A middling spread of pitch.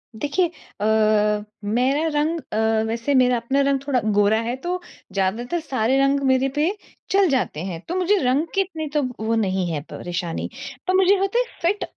No: wide, 7.3 semitones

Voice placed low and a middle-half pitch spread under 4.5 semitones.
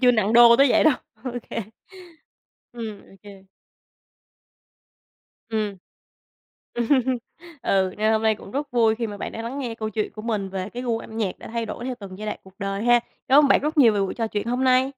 No: high, 225 Hz; average, 2.9 semitones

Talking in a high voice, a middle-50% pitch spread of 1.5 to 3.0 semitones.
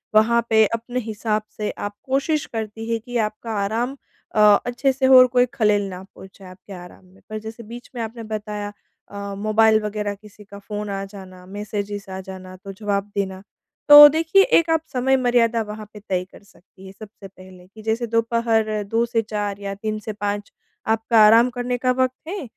Yes: high, 215 Hz; average, 2.7 semitones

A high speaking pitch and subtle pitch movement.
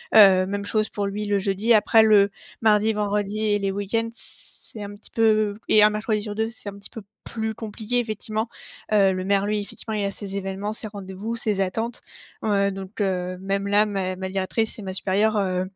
Yes: high, 205 Hz; narrow, 1.7 semitones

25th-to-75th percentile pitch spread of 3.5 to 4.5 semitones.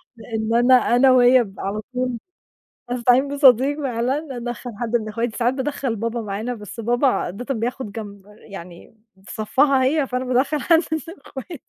No: average, 3.0 semitones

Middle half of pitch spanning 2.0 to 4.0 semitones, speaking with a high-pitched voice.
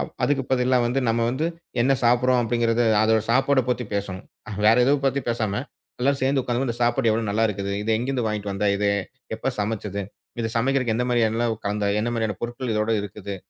No: average, 2.9 semitones; low, 115 Hz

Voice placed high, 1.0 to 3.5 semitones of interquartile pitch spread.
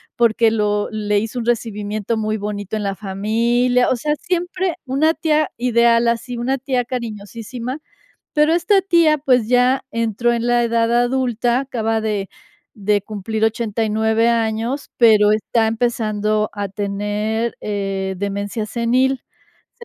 Yes: high, 230 Hz; average, 2.8 semitones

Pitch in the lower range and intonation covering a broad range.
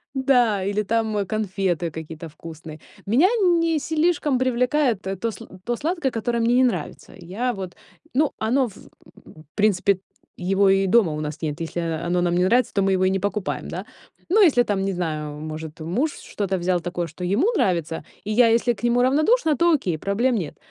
No: high, 200 Hz; wide, 6.0 semitones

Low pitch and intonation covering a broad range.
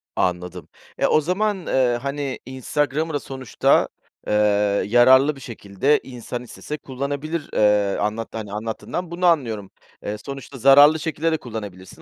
Yes: low, 130 Hz; wide, 5.8 semitones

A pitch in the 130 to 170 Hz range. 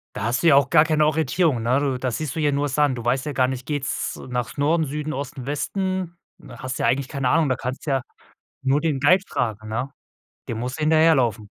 Yes: medium, 140 Hz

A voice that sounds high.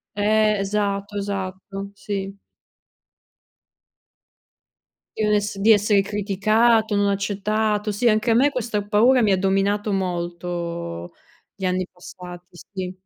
Yes: high, 200 Hz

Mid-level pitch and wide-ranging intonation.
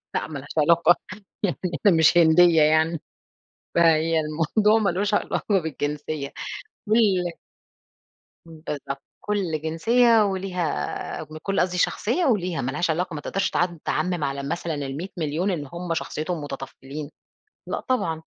No: medium, 165 Hz; average, 3.3 semitones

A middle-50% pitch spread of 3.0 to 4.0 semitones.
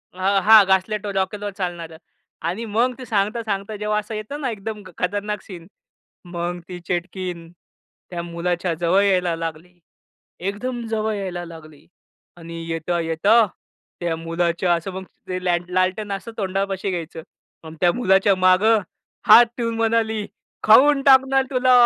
Yes: average, 3.7 semitones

